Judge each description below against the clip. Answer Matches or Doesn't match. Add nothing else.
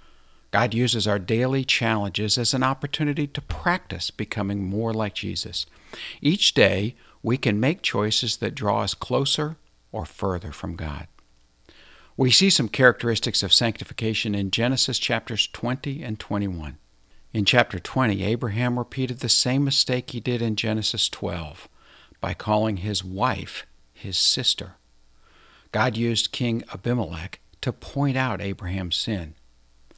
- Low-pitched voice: Matches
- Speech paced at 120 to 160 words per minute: Matches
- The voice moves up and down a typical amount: Matches